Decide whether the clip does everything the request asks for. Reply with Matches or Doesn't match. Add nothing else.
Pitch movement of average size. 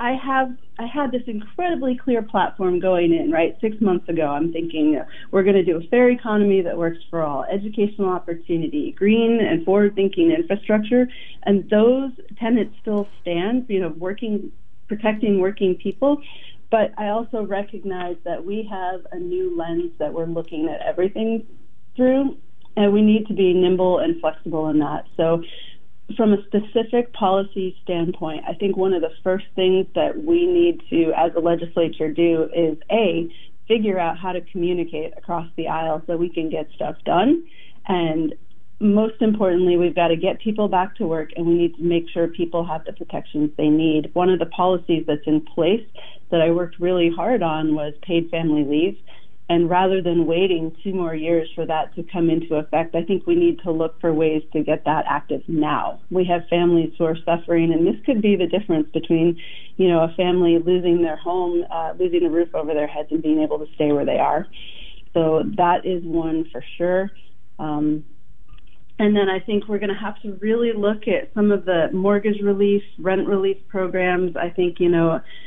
Matches